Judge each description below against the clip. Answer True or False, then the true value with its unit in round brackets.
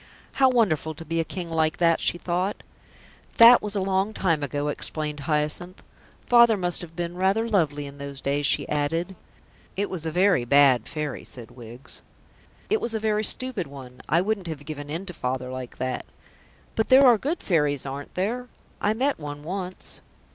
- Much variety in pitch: True (5.7 semitones)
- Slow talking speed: False (185 wpm)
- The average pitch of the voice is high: False (165 Hz)